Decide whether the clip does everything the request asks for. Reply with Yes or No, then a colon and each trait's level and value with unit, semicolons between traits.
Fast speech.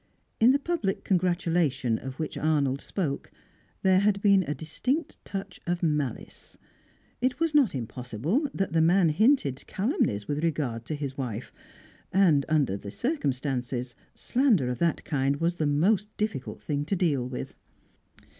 No: average, 150 wpm